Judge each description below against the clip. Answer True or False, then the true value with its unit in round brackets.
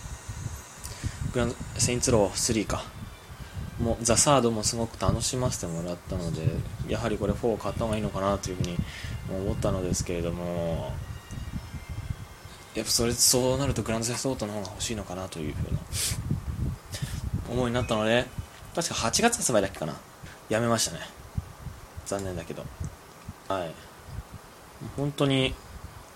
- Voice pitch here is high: False (110 Hz)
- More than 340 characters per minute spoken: False (305 characters per minute)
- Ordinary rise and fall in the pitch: True (4.0 semitones)